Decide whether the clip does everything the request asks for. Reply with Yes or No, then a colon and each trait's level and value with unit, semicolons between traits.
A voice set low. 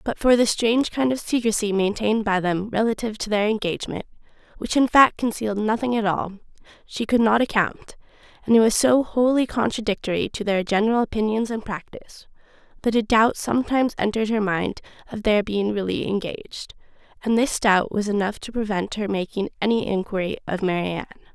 No: high, 215 Hz